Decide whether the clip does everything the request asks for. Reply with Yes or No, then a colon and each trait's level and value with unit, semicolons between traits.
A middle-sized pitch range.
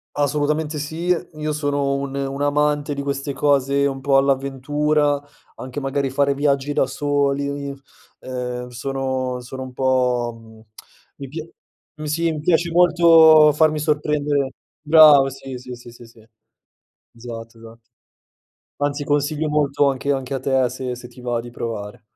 No: narrow, 2.3 semitones